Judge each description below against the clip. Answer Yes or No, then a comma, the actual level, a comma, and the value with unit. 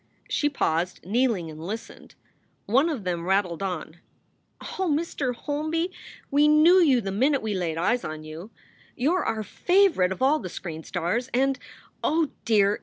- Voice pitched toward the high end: Yes, high, 230 Hz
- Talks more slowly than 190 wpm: Yes, average, 170 wpm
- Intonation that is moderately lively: No, wide, 8.4 semitones